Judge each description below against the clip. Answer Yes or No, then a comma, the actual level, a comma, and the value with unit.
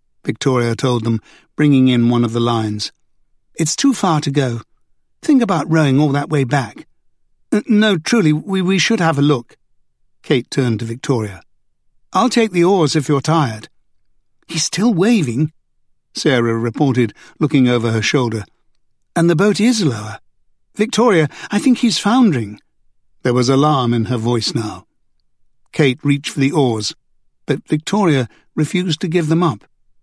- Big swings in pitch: Yes, wide, 6.3 semitones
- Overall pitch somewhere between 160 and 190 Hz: No, medium, 145 Hz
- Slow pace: No, average, 160 wpm